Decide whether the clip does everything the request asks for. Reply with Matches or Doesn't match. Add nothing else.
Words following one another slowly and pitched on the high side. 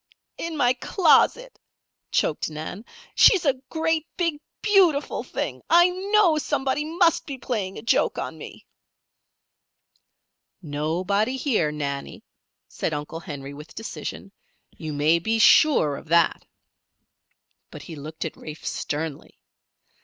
Matches